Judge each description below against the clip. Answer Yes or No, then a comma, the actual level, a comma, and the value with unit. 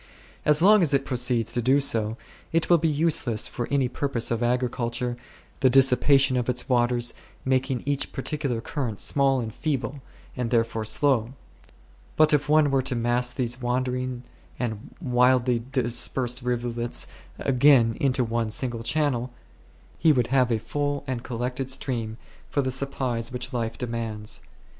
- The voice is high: No, low, 125 Hz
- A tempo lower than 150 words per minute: No, average, 155 wpm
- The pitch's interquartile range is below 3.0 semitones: Yes, narrow, 2.5 semitones